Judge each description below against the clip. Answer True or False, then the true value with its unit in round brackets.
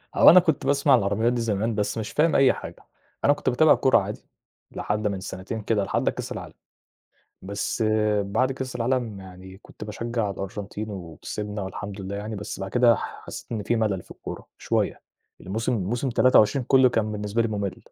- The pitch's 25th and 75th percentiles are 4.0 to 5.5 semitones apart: False (3.4 semitones)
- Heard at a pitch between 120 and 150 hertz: False (110 Hz)